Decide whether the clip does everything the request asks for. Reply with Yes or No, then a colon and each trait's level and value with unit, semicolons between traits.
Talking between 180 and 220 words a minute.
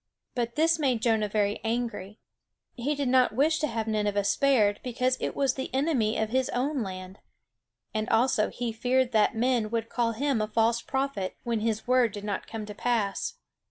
Yes: average, 190 wpm